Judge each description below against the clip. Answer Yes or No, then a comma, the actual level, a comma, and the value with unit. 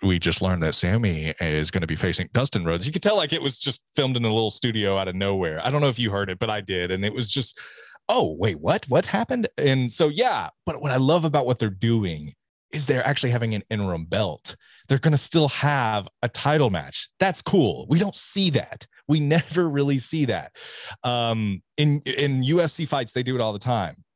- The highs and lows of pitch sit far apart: Yes, wide, 6.6 semitones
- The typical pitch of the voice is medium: No, low, 125 Hz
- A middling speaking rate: No, fast, 235 wpm